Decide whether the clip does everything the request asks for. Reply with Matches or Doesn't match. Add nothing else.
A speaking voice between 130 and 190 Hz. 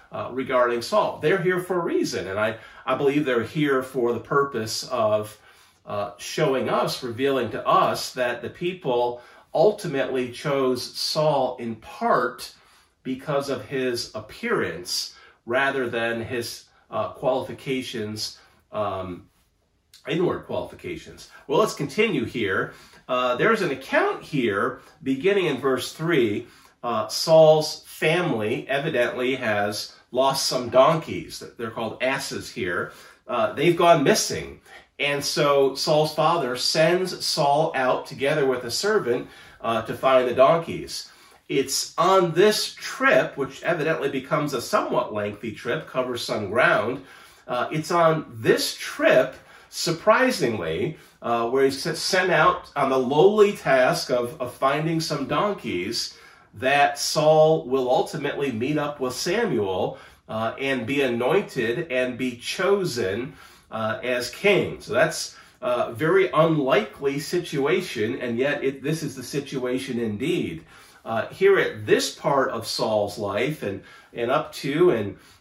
Matches